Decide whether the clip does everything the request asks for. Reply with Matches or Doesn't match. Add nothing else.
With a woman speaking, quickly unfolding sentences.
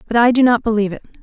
Matches